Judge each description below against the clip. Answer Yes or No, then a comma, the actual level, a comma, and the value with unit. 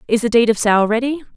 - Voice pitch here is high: Yes, high, 235 Hz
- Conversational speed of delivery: No, fast, 265 wpm